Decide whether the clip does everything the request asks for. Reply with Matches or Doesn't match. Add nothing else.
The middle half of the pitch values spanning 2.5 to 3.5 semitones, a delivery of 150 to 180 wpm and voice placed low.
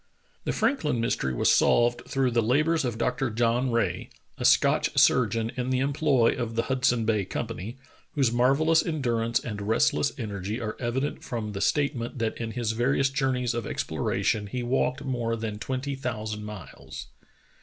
Matches